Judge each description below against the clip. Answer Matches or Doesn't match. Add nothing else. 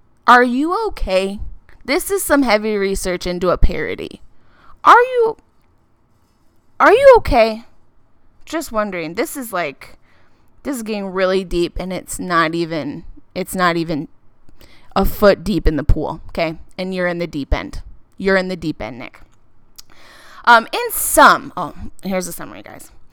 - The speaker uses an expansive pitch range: Matches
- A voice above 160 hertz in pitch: Matches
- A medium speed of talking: Matches